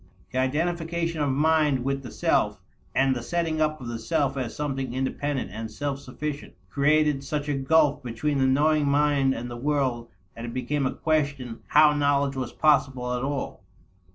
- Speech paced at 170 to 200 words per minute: Yes, average, 180 wpm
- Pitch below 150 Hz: Yes, medium, 140 Hz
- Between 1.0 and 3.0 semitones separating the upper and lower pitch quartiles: Yes, narrow, 2.6 semitones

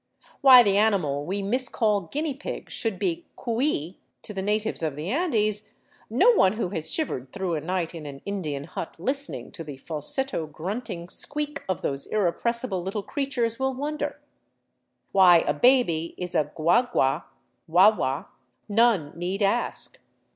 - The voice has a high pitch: Yes, high, 200 Hz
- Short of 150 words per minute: No, average, 155 wpm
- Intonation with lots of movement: Yes, wide, 6.6 semitones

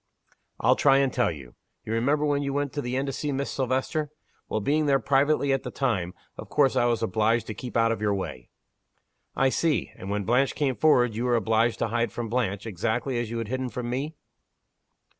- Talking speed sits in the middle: No, fast, 220 wpm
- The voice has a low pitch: Yes, low, 125 Hz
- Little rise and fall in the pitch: No, average, 3.5 semitones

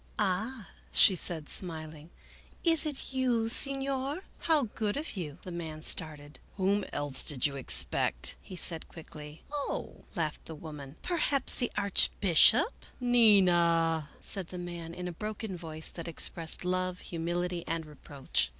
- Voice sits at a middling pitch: Yes, medium, 175 Hz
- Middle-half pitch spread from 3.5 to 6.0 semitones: Yes, wide, 5.6 semitones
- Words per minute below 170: No, average, 175 wpm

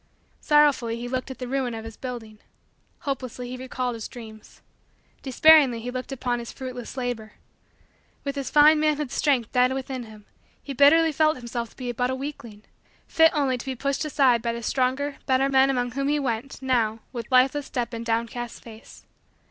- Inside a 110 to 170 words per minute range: No, average, 185 wpm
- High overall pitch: Yes, very high, 255 Hz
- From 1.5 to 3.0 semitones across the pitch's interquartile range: Yes, average, 2.7 semitones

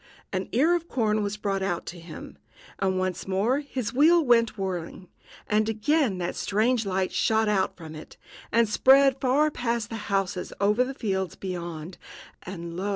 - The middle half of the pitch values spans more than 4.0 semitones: Yes, average, 4.9 semitones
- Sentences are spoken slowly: No, average, 165 wpm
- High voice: Yes, high, 210 Hz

